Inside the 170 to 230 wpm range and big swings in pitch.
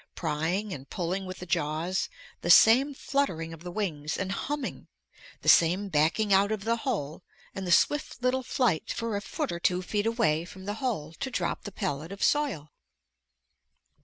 Yes: average, 180 wpm; wide, 5.7 semitones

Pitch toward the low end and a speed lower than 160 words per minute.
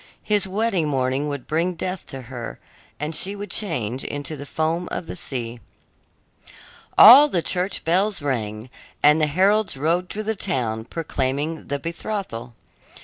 No: medium, 160 Hz; average, 150 wpm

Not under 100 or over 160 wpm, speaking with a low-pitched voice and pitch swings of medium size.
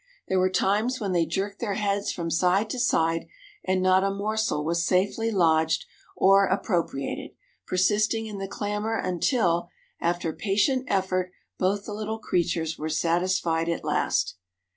No: average, 145 wpm; high, 190 Hz; average, 3.4 semitones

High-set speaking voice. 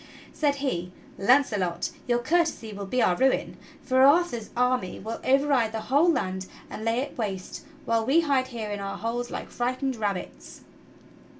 Yes: high, 240 Hz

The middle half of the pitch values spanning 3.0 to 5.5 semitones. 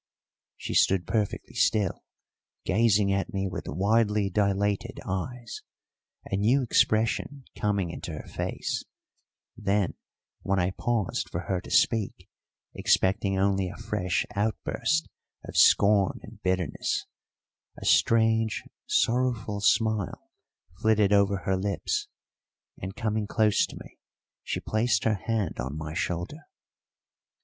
No: narrow, 2.5 semitones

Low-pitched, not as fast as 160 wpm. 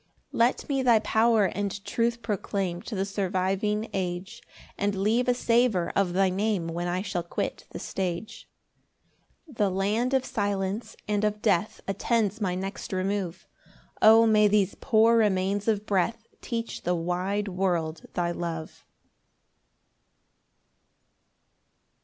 No: high, 200 Hz; average, 140 wpm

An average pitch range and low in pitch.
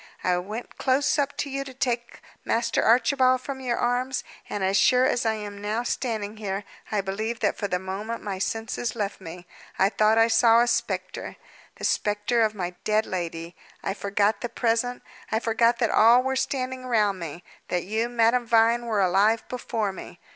No: average, 3.2 semitones; high, 225 Hz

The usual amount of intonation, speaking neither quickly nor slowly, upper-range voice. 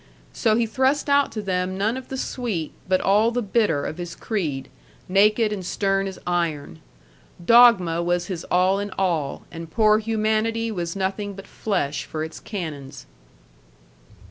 Yes: average, 4.2 semitones; average, 160 wpm; high, 195 Hz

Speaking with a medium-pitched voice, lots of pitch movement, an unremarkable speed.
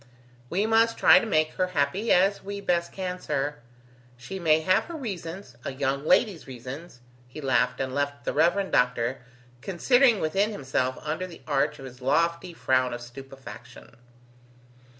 Yes: medium, 155 Hz; wide, 6.0 semitones; average, 160 wpm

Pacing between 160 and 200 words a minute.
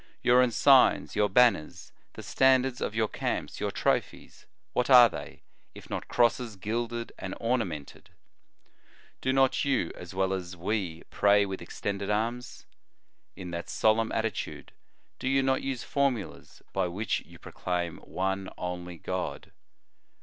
No: average, 145 wpm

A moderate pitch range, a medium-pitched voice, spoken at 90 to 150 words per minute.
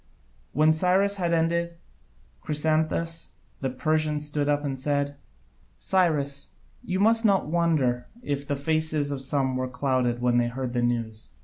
Yes: average, 3.8 semitones; medium, 145 Hz; average, 145 wpm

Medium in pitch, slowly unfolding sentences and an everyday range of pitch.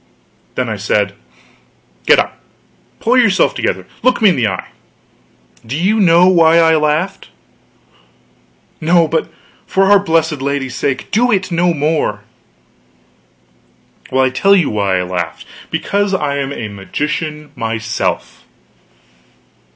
No: medium, 155 Hz; slow, 130 wpm; wide, 6.9 semitones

